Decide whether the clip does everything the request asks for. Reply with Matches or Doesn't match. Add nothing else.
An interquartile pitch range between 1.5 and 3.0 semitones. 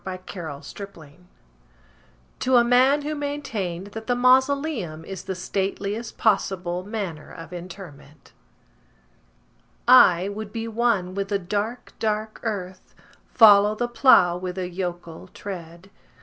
Doesn't match